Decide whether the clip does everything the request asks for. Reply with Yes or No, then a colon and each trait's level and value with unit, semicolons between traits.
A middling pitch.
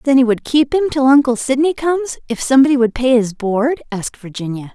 No: very high, 260 Hz